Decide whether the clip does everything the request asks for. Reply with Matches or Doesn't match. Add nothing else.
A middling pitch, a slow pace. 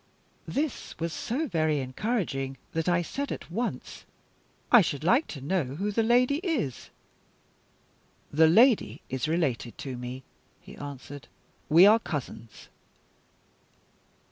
Matches